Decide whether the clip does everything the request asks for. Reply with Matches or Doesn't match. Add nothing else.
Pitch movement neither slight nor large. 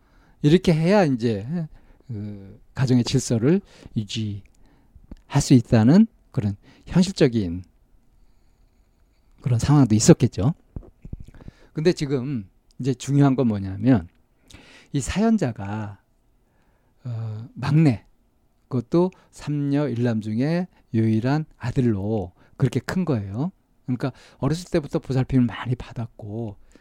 Matches